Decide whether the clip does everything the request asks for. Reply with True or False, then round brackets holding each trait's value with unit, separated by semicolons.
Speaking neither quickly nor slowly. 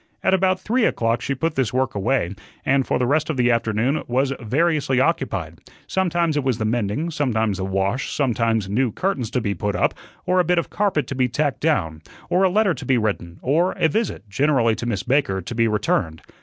False (215 wpm)